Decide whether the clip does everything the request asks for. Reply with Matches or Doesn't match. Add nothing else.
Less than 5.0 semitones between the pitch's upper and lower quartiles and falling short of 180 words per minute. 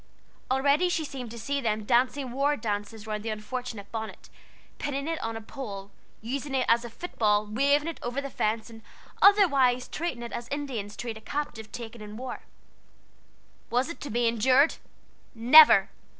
Matches